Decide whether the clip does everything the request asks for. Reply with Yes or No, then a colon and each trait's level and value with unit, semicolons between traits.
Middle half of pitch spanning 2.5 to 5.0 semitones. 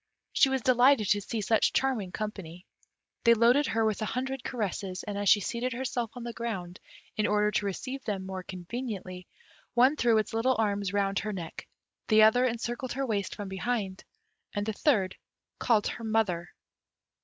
Yes: average, 3.6 semitones